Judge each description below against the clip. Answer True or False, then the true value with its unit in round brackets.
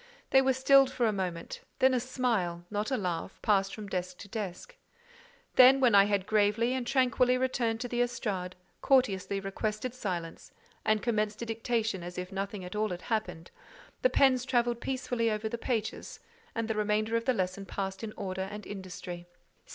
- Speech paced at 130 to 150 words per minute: False (170 wpm)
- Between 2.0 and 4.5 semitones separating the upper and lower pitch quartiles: True (4.2 semitones)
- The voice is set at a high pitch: True (215 Hz)